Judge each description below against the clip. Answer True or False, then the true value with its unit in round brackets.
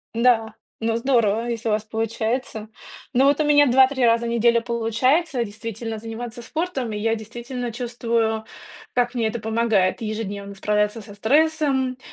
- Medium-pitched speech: False (230 Hz)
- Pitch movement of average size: False (2.2 semitones)